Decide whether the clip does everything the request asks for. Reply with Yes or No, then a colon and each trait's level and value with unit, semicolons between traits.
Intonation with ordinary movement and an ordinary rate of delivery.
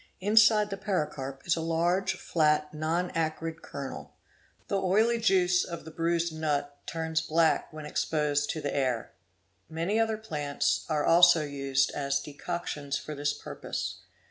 Yes: average, 3.4 semitones; average, 150 wpm